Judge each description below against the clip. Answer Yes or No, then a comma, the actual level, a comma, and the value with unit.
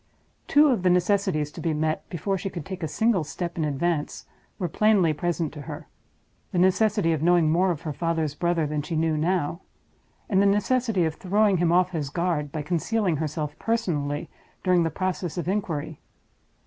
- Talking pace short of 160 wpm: No, average, 185 wpm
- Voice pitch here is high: No, medium, 175 Hz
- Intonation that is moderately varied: Yes, average, 3.4 semitones